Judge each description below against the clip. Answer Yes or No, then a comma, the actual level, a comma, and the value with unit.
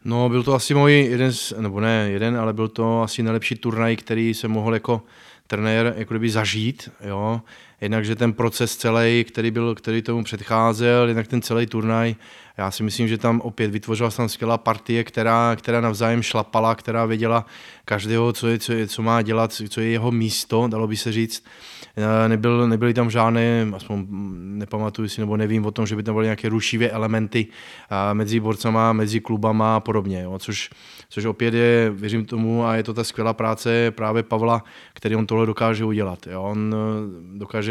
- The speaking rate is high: Yes, fast, 185 wpm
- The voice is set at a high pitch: No, low, 115 Hz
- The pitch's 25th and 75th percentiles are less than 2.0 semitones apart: Yes, narrow, 1.1 semitones